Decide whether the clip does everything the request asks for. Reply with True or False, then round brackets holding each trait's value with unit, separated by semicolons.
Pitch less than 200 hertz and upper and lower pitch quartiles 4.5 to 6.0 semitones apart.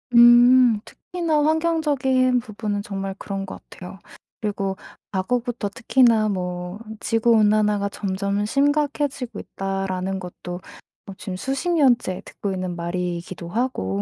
False (210 Hz; 5.1 semitones)